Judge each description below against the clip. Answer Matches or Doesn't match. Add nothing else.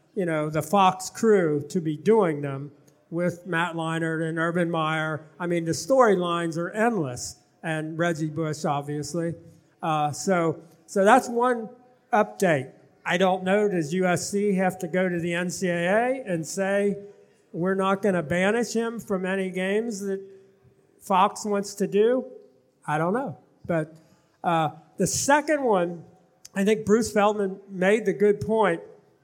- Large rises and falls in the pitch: Doesn't match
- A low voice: Doesn't match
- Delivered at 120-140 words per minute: Doesn't match